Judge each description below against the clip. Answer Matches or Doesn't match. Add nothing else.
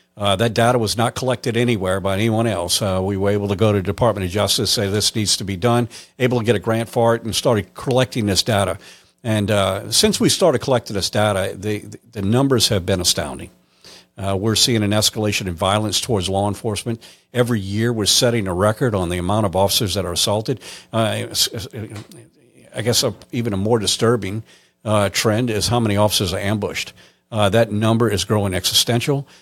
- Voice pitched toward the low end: Matches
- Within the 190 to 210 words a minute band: Matches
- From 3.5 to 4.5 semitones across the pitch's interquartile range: Doesn't match